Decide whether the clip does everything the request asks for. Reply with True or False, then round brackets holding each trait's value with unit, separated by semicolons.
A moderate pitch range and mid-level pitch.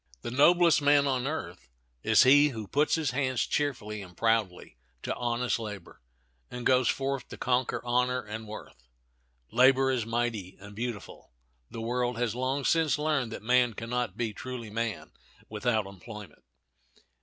False (3.3 semitones; 120 Hz)